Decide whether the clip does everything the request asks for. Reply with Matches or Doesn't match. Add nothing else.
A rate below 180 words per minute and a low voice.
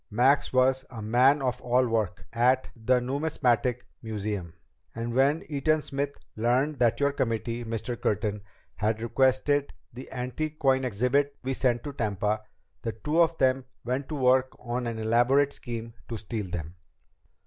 Matches